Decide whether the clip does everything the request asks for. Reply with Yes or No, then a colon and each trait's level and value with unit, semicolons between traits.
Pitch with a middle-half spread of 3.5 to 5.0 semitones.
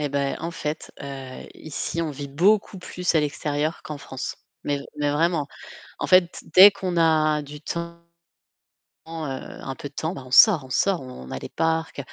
No: average, 3.1 semitones